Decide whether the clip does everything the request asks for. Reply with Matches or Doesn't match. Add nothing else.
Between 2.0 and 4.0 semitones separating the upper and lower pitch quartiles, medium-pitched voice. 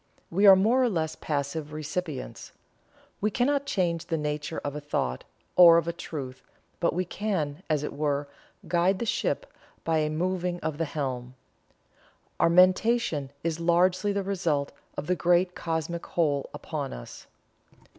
Matches